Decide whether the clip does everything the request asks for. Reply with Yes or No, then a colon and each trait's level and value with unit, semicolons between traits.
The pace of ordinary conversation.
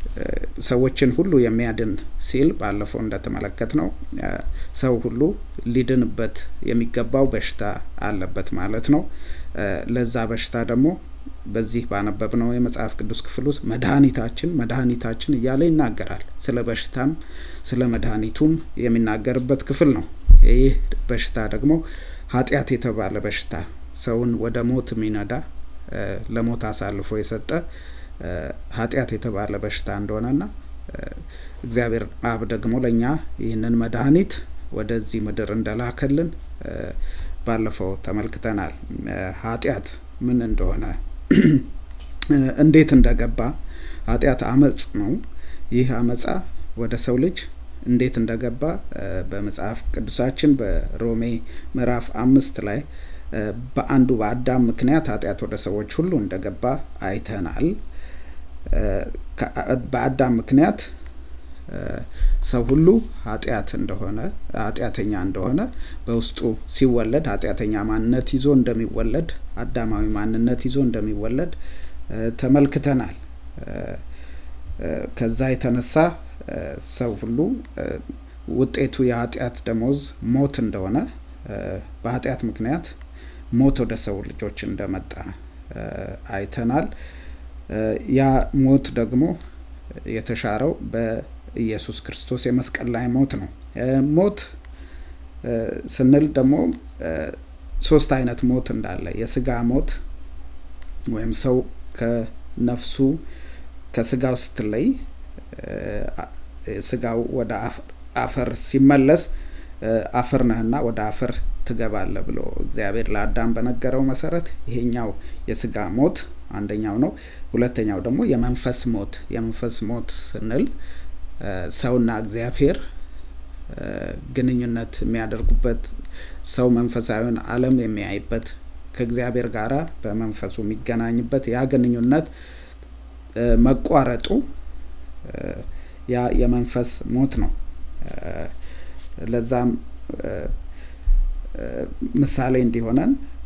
No: slow, 85 wpm